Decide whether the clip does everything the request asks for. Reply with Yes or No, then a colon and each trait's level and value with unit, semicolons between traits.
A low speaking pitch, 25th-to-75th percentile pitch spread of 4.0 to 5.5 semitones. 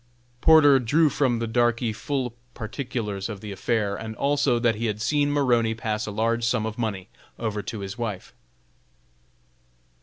No: low, 115 Hz; average, 2.7 semitones